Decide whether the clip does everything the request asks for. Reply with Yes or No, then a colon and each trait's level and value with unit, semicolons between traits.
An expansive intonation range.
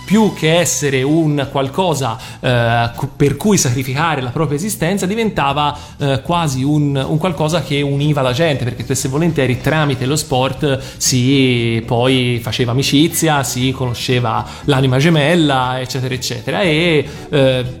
No: average, 3.3 semitones